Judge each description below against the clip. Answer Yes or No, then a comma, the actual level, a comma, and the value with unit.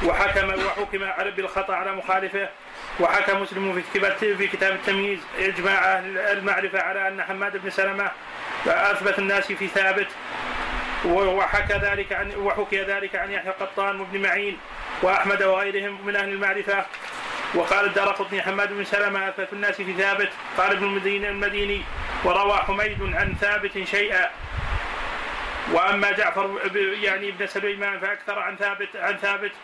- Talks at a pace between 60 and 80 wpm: No, average, 130 wpm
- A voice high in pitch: Yes, high, 200 Hz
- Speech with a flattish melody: Yes, narrow, 0.7 semitones